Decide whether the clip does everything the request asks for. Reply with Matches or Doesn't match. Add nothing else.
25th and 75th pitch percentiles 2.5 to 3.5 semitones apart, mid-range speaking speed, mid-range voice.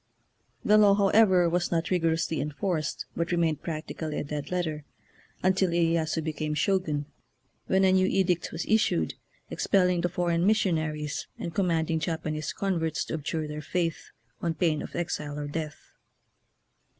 Matches